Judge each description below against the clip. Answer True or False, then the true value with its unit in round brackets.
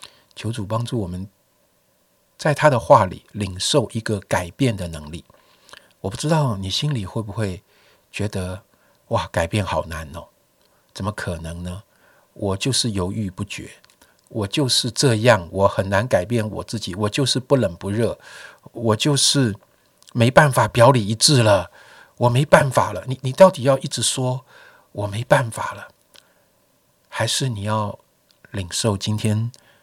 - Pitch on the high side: False (110 Hz)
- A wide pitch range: False (4.5 semitones)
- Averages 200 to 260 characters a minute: True (215 characters per minute)